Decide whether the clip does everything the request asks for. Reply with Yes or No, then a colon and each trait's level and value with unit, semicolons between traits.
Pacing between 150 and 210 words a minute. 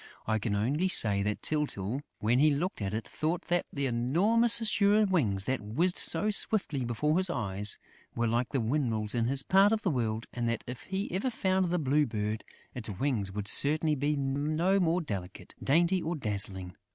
Yes: average, 190 wpm